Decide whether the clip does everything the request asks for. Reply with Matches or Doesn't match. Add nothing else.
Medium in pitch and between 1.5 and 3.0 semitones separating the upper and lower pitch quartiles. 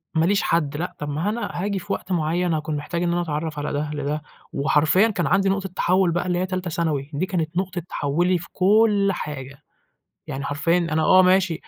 Doesn't match